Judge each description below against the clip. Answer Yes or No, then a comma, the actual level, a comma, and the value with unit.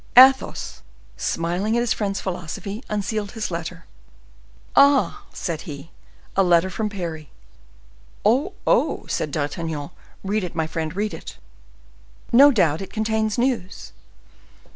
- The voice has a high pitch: Yes, high, 195 Hz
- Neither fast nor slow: No, slow, 125 wpm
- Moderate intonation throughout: Yes, average, 4.8 semitones